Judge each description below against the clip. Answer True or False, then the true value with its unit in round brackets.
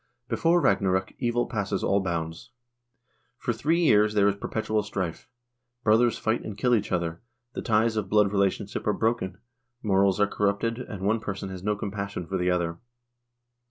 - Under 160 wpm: False (165 wpm)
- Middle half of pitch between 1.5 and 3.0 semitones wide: True (2.5 semitones)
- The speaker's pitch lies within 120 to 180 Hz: False (100 Hz)